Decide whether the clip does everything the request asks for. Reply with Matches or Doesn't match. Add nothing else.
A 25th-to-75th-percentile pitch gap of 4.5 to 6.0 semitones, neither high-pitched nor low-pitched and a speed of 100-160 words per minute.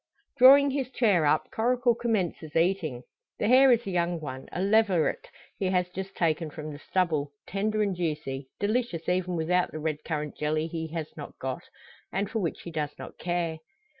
Doesn't match